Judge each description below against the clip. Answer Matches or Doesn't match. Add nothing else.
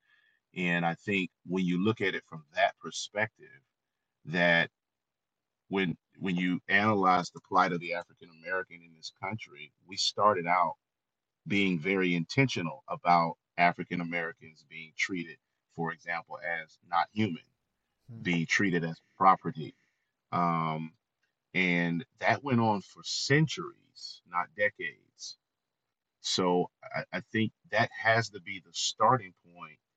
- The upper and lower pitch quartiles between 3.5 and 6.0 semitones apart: Matches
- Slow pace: Matches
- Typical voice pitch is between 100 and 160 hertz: Doesn't match